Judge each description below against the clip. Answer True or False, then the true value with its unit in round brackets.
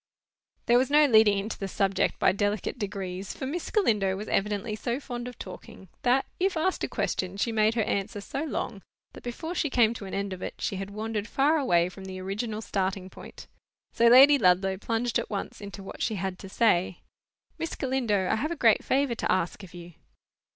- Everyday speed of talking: False (210 wpm)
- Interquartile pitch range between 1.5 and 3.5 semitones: False (4.2 semitones)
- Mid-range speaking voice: False (210 Hz)